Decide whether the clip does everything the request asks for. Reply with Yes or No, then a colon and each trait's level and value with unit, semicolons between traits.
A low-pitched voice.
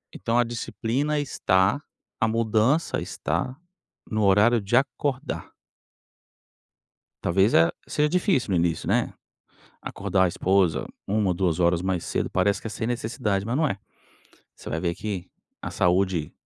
Yes: low, 105 Hz